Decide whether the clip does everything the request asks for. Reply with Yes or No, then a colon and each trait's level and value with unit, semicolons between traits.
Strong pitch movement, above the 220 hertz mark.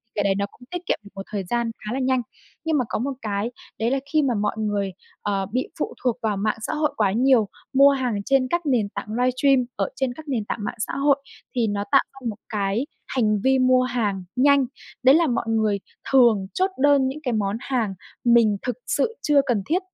No: average, 4.3 semitones; high, 245 Hz